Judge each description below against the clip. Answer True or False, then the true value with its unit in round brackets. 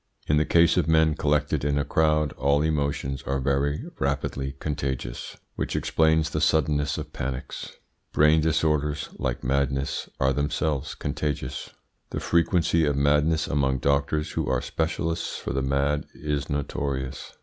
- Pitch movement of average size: False (2.1 semitones)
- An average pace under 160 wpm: True (145 wpm)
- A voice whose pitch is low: True (75 Hz)